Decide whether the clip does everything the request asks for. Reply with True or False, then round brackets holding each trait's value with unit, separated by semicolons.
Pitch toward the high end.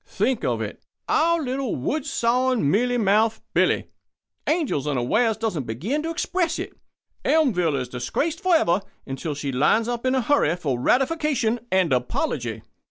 True (230 Hz)